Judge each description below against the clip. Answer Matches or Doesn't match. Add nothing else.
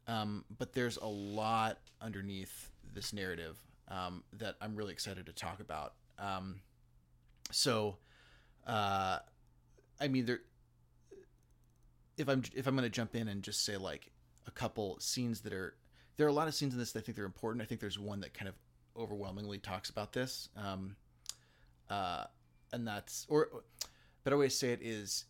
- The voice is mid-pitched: Doesn't match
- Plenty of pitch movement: Matches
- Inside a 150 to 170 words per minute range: Doesn't match